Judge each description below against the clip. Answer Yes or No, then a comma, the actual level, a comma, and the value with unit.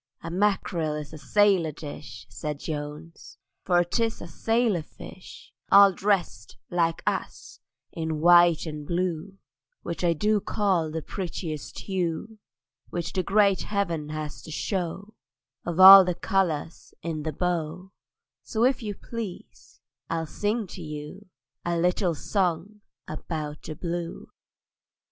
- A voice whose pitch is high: No, medium, 175 Hz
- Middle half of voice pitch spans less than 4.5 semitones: Yes, average, 3.8 semitones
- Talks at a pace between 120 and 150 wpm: Yes, slow, 135 wpm